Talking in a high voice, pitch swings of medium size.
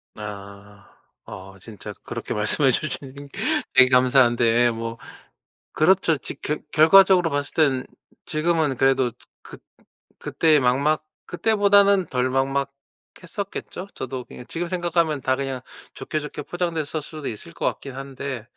No: medium, 140 Hz; average, 4.5 semitones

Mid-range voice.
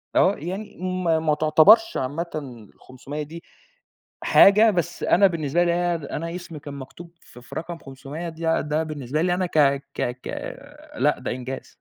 Yes: medium, 160 Hz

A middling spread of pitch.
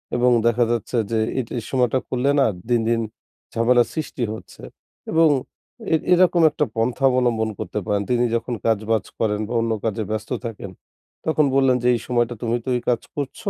No: narrow, 2.3 semitones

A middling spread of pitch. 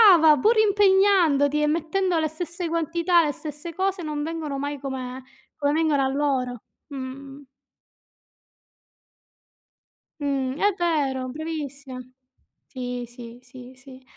Yes: average, 3.9 semitones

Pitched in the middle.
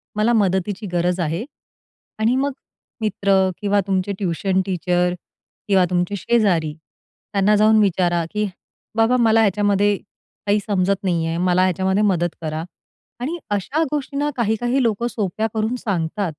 No: high, 200 Hz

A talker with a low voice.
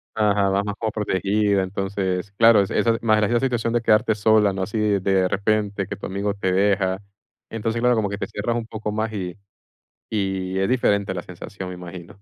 Yes: low, 100 Hz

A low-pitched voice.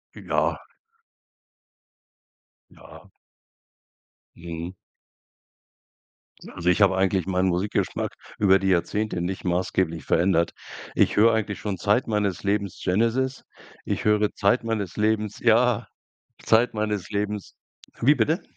Yes: low, 100 Hz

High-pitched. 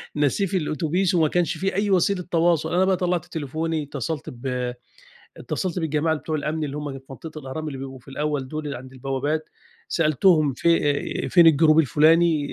No: medium, 155 Hz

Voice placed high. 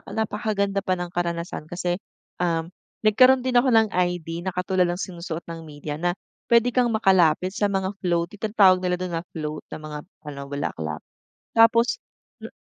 No: medium, 180 Hz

